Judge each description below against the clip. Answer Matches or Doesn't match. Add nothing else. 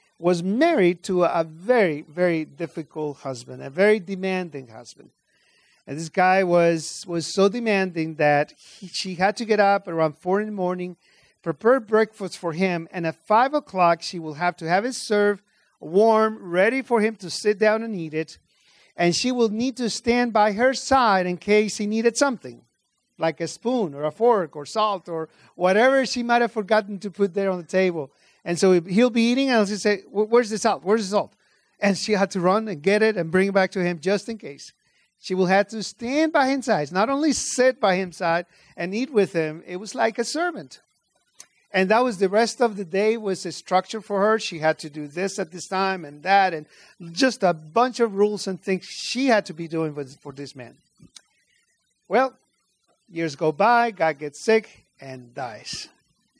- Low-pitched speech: Doesn't match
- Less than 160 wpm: Doesn't match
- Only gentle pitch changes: Doesn't match